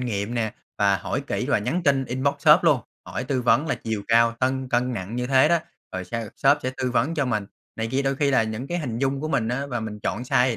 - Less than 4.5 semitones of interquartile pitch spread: Yes, average, 3.3 semitones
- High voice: No, low, 125 Hz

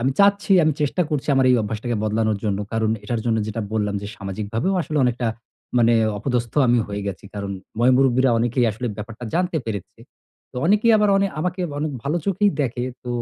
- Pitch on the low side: Yes, low, 120 Hz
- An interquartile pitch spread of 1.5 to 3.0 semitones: No, wide, 5.6 semitones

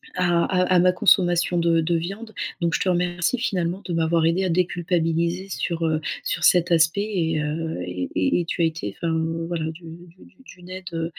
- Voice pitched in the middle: Yes, medium, 170 Hz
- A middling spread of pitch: No, narrow, 1.8 semitones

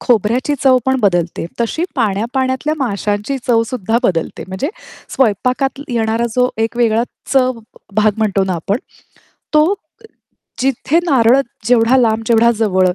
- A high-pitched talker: Yes, high, 230 Hz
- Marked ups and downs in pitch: No, average, 3.4 semitones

